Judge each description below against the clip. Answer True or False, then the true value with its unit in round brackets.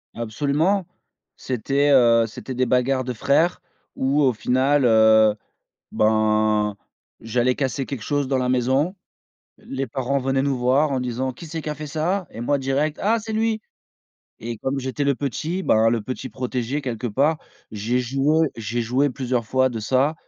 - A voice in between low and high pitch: False (130 Hz)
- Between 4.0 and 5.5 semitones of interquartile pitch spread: False (3.3 semitones)